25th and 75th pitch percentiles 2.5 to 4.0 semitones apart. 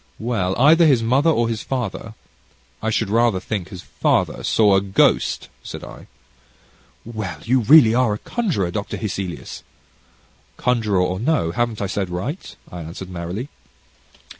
No: average, 4.5 semitones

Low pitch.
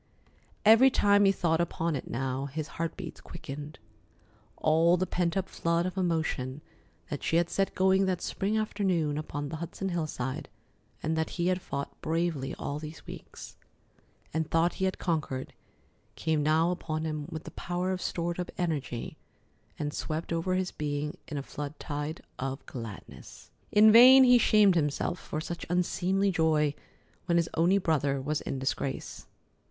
No: medium, 165 Hz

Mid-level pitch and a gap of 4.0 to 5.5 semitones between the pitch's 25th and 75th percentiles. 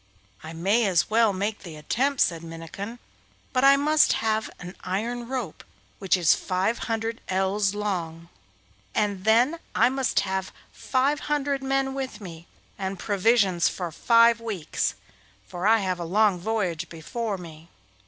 No: high, 205 Hz; average, 4.6 semitones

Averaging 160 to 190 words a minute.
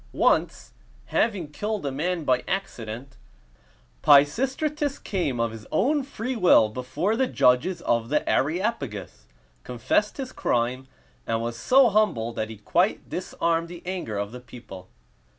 No: average, 140 wpm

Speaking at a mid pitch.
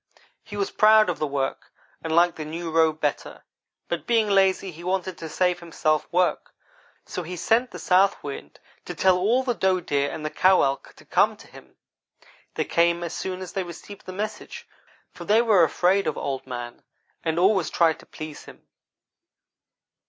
Yes: medium, 175 Hz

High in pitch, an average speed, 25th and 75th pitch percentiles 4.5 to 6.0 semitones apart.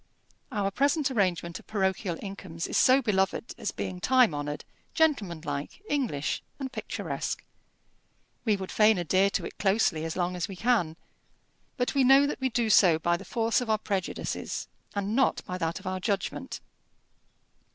Yes: high, 195 Hz; average, 160 wpm; wide, 5.6 semitones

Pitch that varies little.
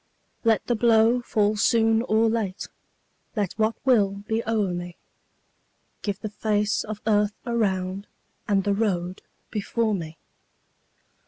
Yes: narrow, 2.2 semitones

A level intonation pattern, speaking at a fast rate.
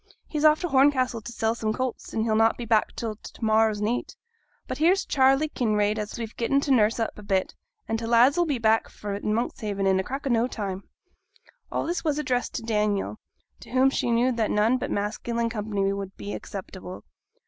No: average, 3.5 semitones; fast, 210 wpm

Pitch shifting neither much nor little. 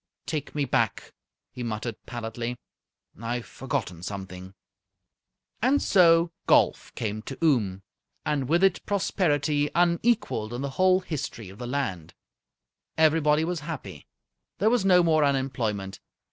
No: wide, 7.0 semitones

